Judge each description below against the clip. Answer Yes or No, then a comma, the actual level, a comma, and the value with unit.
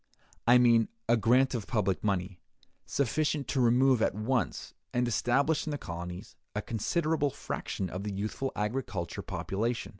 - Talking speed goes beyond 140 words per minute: Yes, average, 150 wpm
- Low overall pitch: Yes, low, 115 Hz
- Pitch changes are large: No, average, 4.7 semitones